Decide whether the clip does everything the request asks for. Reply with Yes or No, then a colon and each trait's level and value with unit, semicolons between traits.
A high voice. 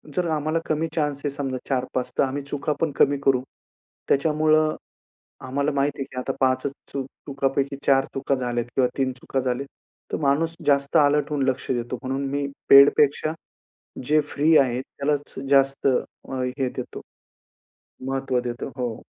No: medium, 140 Hz